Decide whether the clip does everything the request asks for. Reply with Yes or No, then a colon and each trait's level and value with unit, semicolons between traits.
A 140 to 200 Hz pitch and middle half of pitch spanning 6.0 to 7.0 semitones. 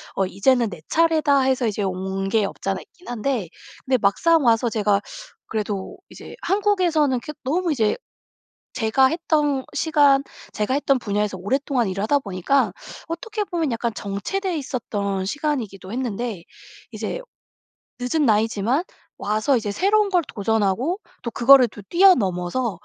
No: high, 245 Hz; wide, 6.4 semitones